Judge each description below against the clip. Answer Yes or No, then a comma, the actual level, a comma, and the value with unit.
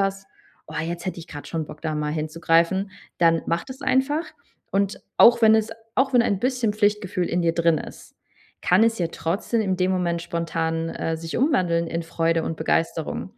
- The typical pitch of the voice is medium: Yes, medium, 175 Hz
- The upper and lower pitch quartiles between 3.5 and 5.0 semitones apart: Yes, average, 4.2 semitones